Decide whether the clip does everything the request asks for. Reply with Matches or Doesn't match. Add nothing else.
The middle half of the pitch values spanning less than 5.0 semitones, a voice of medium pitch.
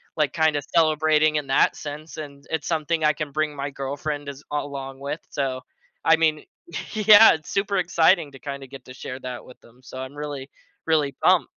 Matches